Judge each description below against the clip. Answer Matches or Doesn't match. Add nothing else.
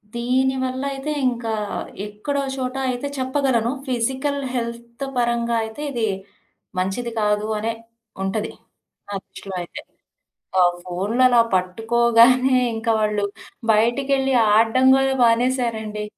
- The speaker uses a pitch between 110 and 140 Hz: Doesn't match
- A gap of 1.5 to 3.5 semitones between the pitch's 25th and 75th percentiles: Matches